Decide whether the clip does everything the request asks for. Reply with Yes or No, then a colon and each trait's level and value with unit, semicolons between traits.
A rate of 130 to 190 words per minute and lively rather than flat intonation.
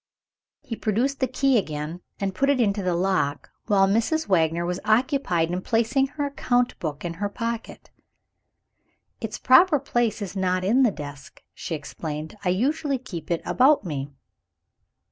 Yes: average, 160 wpm; wide, 6.8 semitones